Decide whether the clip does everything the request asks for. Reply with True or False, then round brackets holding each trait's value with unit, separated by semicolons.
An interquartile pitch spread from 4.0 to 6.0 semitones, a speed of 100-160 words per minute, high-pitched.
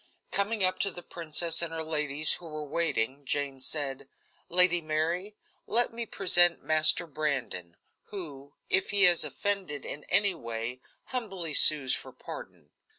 False (4.4 semitones; 150 wpm; 160 Hz)